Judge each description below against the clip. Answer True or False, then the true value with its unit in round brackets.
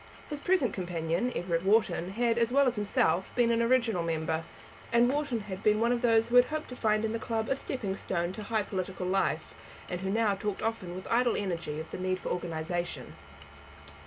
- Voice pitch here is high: True (210 Hz)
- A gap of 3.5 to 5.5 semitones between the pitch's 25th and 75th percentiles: True (4.5 semitones)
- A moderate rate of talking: False (210 wpm)